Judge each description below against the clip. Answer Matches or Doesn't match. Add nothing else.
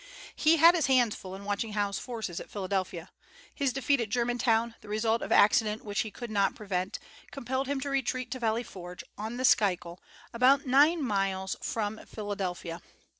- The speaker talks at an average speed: Matches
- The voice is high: Matches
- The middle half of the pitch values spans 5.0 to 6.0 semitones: Doesn't match